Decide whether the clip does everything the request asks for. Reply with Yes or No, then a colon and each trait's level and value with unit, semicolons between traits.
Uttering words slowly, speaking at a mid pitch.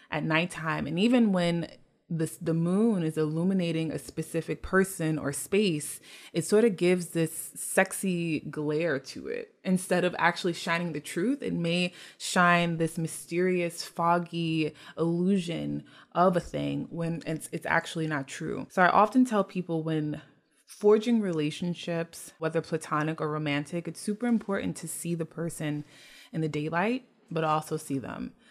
No: average, 150 wpm; medium, 165 Hz